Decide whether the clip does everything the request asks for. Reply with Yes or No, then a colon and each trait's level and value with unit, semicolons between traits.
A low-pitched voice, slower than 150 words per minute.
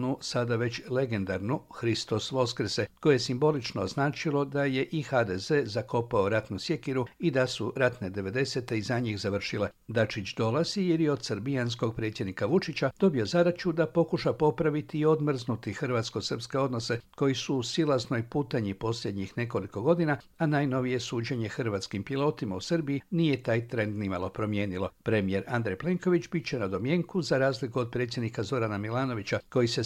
No: low, 125 Hz; average, 155 wpm